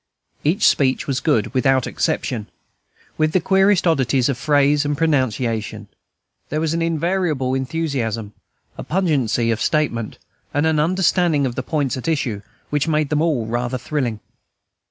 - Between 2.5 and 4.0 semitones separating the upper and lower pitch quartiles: No, average, 4.5 semitones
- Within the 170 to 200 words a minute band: No, average, 150 wpm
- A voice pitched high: No, medium, 145 Hz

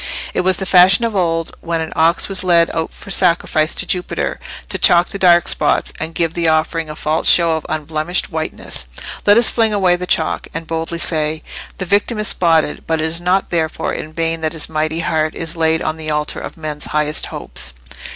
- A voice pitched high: No, medium, 165 Hz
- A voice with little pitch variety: Yes, narrow, 2.2 semitones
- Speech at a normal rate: No, fast, 210 wpm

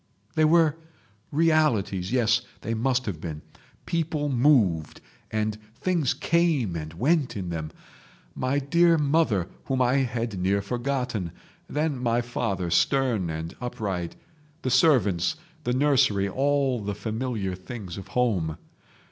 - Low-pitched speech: Yes, low, 120 Hz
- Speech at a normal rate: No, slow, 125 wpm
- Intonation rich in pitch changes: Yes, wide, 6.3 semitones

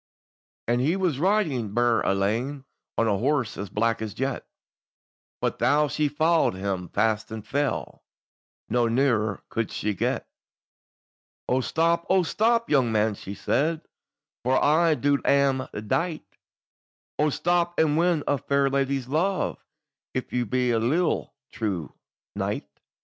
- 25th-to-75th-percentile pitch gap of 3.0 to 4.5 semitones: No, wide, 5.6 semitones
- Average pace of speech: Yes, average, 145 wpm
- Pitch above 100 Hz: Yes, low, 135 Hz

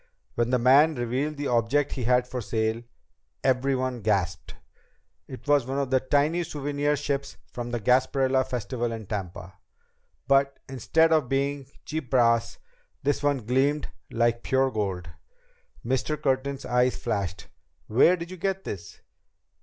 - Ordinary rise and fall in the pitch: Yes, average, 3.3 semitones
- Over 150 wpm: No, average, 145 wpm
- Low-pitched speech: Yes, low, 130 Hz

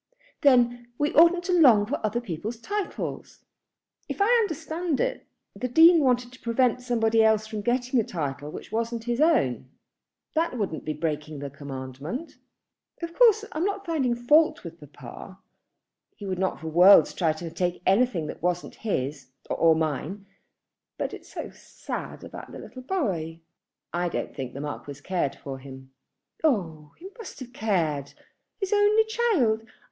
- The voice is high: Yes, high, 220 Hz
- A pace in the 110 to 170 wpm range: Yes, average, 160 wpm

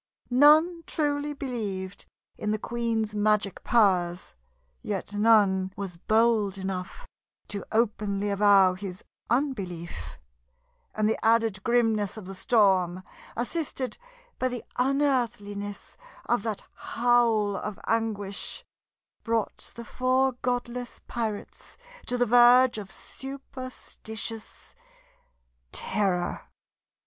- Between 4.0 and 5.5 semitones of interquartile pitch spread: No, average, 3.6 semitones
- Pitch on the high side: Yes, high, 220 Hz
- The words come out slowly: Yes, slow, 100 wpm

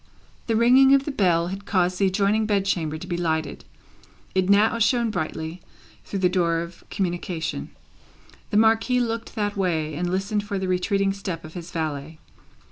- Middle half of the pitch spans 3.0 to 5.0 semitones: Yes, average, 3.9 semitones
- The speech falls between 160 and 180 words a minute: Yes, average, 175 wpm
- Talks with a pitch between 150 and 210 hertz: Yes, high, 190 Hz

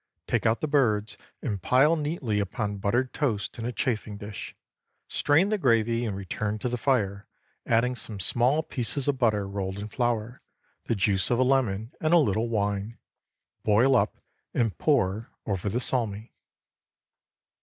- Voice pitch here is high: No, low, 115 Hz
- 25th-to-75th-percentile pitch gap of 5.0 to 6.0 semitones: No, average, 3.9 semitones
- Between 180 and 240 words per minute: No, average, 160 wpm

